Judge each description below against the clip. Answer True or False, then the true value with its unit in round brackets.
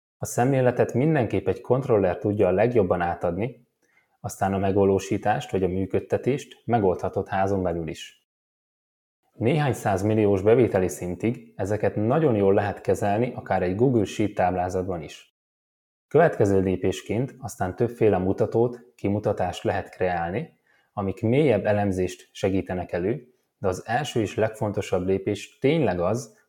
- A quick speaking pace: False (125 wpm)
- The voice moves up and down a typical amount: True (3.6 semitones)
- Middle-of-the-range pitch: False (100 Hz)